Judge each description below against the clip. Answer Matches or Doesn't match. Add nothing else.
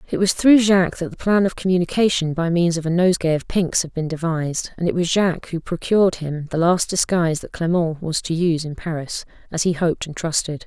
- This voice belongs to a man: Doesn't match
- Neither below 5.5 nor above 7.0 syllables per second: Matches